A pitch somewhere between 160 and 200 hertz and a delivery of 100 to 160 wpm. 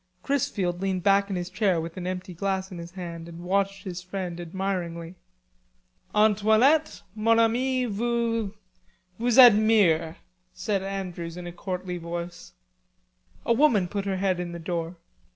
Yes: high, 190 Hz; average, 150 wpm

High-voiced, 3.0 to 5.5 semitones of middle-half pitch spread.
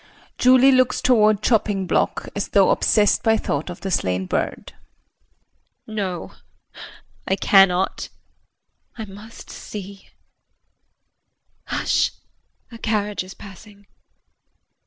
No: high, 205 Hz; narrow, 2.4 semitones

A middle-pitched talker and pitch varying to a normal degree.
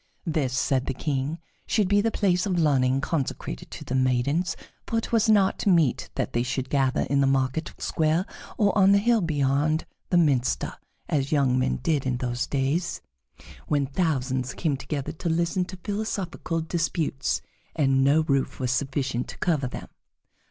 Yes: medium, 145 Hz; average, 4.7 semitones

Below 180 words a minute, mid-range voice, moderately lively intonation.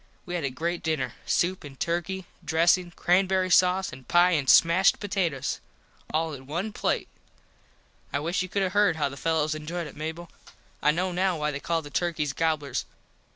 No: average, 185 wpm; medium, 170 Hz; average, 3.3 semitones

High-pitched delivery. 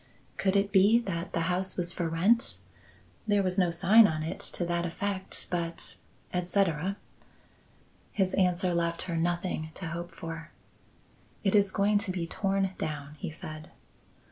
No: medium, 180 Hz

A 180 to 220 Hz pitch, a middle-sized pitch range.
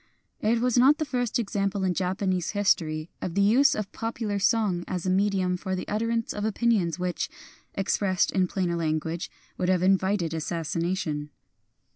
Yes: high, 190 Hz; average, 3.4 semitones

